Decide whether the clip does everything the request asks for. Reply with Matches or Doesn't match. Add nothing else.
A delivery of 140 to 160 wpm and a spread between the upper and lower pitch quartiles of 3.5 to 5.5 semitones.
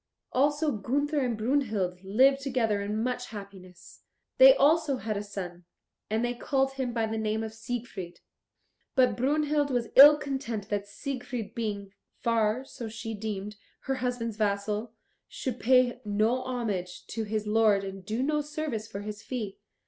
Matches